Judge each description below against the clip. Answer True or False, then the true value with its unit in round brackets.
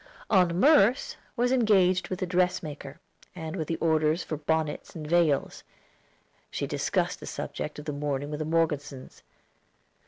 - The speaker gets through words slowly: False (150 wpm)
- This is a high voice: False (165 Hz)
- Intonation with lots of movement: False (3.5 semitones)